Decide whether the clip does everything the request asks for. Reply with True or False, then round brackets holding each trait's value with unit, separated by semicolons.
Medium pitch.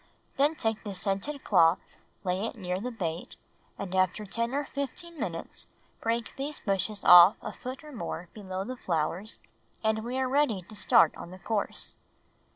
False (215 Hz)